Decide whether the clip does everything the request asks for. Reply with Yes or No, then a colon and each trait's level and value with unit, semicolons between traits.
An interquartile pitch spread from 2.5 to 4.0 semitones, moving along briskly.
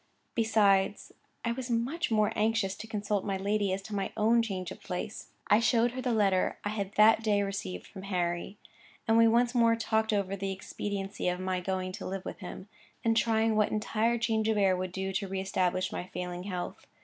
Yes: average, 2.8 semitones; fast, 210 wpm